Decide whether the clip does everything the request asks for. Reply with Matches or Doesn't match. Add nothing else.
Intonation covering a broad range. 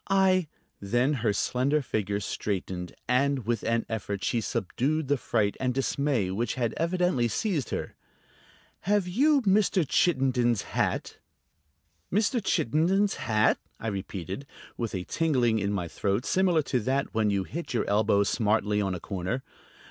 Matches